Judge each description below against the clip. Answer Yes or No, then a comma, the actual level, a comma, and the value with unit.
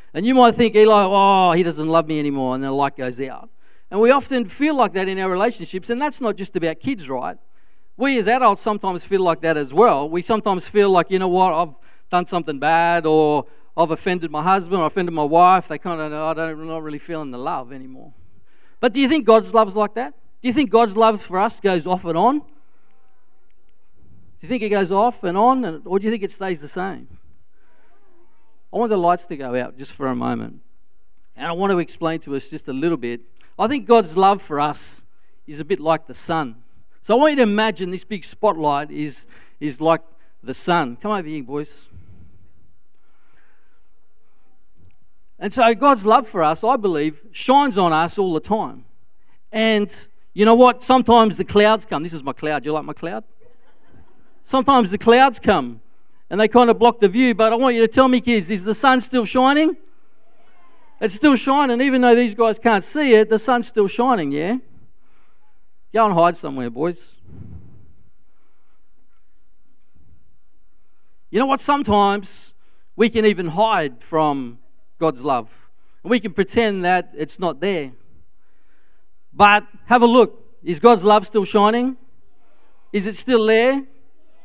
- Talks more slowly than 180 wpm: No, average, 190 wpm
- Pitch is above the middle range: Yes, high, 200 Hz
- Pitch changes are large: Yes, wide, 6.4 semitones